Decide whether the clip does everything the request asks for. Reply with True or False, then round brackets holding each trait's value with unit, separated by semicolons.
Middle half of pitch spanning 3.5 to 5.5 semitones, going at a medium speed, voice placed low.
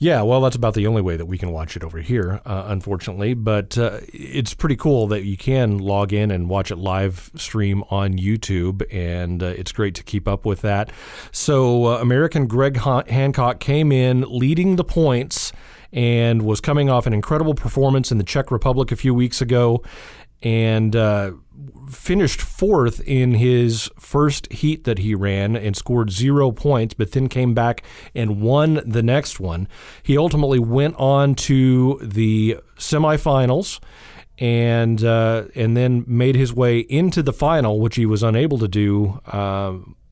True (4.3 semitones; 170 wpm; 120 Hz)